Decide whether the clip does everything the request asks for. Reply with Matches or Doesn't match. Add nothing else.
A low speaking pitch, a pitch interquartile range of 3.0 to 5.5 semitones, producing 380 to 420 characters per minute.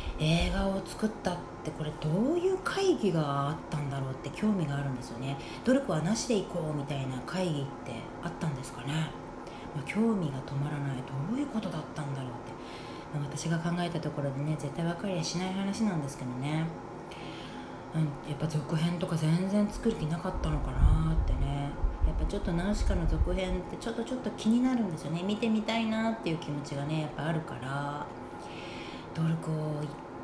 Doesn't match